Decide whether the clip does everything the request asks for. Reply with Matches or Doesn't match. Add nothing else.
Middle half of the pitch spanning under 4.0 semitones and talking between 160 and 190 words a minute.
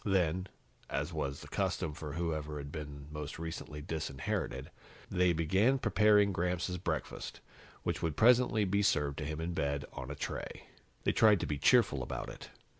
Doesn't match